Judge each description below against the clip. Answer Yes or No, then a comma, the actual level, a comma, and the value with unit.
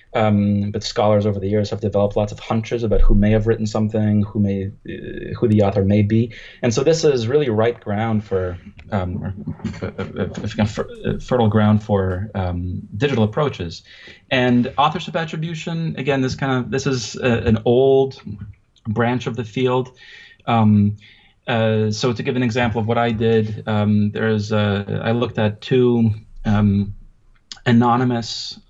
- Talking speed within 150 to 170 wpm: Yes, average, 165 wpm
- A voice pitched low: Yes, low, 110 Hz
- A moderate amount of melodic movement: Yes, average, 3.0 semitones